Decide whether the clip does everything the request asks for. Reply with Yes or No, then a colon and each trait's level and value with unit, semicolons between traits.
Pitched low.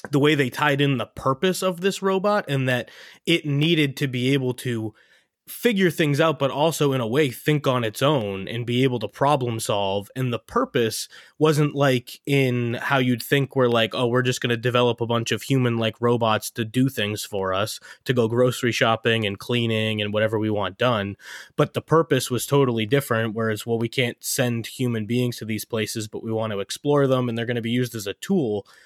Yes: low, 125 Hz